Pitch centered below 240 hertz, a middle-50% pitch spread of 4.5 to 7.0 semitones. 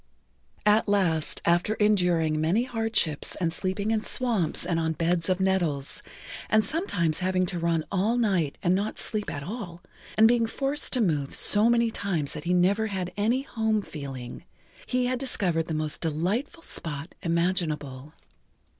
Yes: medium, 185 Hz; average, 5.1 semitones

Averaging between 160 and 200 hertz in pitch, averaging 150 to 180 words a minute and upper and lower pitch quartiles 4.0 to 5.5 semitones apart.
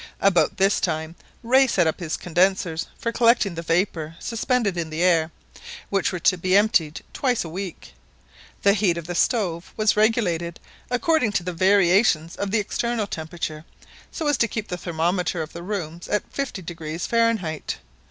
Yes: medium, 185 Hz; average, 170 wpm; average, 4.4 semitones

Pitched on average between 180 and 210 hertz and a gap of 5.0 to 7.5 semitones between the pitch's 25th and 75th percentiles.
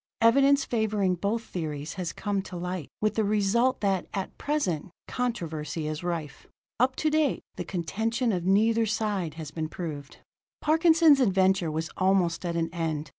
Yes: high, 190 Hz; wide, 5.4 semitones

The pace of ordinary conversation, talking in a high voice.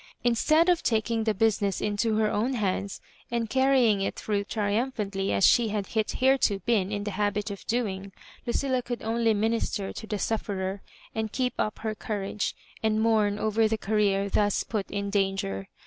Yes: average, 170 wpm; high, 215 Hz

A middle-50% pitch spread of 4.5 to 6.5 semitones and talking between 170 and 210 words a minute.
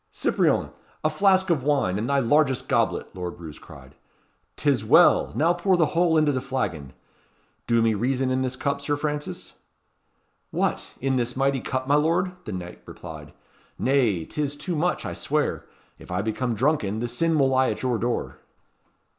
Yes: average, 4.9 semitones; average, 175 wpm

